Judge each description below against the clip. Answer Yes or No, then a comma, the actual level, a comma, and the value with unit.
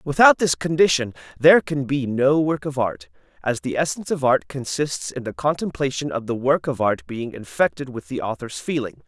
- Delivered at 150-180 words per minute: No, average, 200 wpm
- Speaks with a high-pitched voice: No, low, 135 Hz